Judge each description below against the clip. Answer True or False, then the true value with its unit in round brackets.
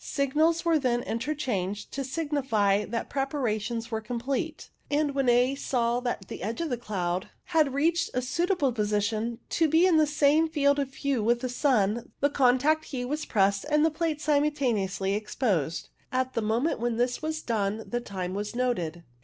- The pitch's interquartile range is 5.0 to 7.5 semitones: True (5.3 semitones)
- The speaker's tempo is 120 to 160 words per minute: False (180 wpm)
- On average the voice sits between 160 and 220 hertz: False (250 Hz)